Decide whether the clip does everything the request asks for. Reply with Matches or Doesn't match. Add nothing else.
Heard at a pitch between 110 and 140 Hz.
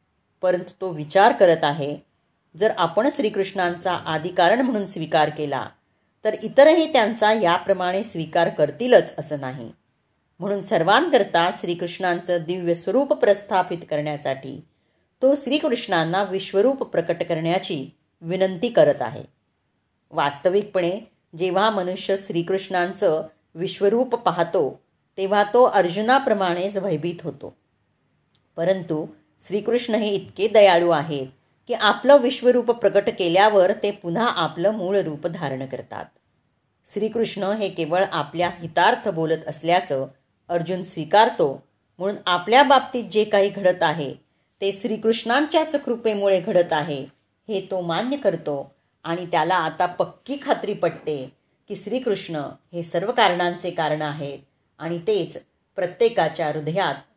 Doesn't match